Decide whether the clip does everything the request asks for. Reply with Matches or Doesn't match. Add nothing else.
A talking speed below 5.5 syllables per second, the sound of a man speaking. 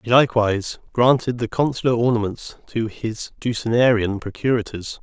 Matches